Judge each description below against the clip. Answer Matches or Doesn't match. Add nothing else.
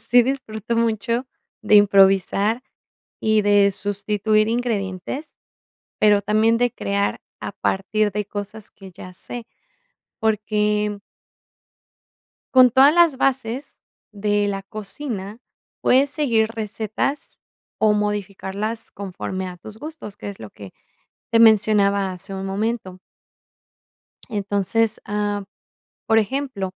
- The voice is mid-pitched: Doesn't match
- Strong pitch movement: Doesn't match